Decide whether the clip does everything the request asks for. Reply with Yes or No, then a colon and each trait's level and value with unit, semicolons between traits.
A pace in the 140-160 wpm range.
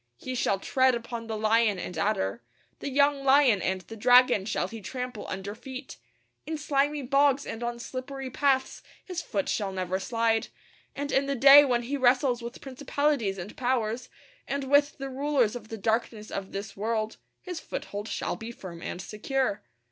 No: average, 180 wpm